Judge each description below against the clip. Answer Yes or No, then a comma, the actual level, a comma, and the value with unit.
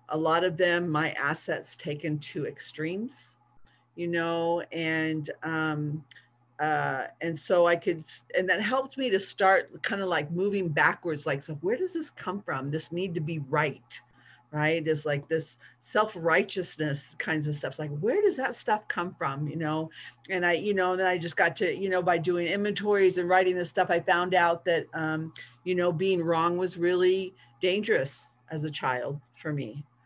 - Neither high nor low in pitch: Yes, medium, 165 Hz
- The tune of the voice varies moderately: Yes, average, 3.3 semitones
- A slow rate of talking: No, average, 190 wpm